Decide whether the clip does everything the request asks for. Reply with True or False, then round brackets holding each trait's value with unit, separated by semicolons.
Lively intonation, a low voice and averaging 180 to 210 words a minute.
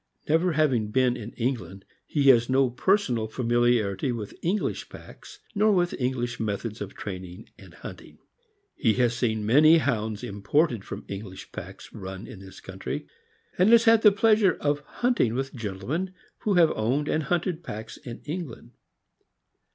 False (6.9 semitones; 125 Hz; 155 wpm)